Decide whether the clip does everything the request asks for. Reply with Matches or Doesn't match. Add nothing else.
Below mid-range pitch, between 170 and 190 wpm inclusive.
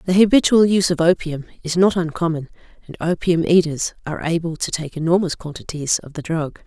Doesn't match